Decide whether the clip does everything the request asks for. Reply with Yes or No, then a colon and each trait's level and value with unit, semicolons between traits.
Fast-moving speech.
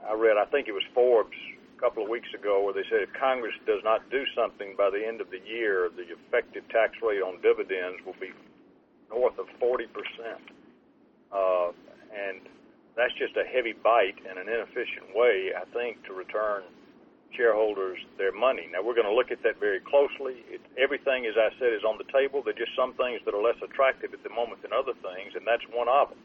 Yes: fast, 215 wpm